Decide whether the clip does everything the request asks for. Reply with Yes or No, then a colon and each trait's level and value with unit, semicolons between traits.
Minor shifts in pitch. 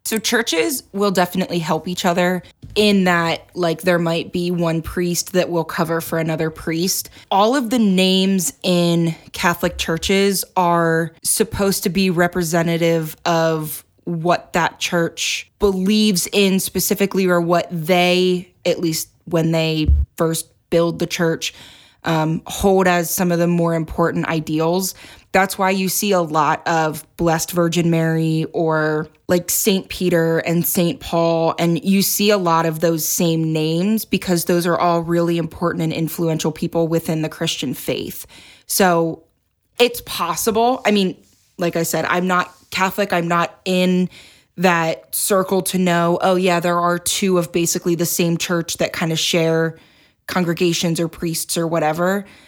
Yes: narrow, 2.0 semitones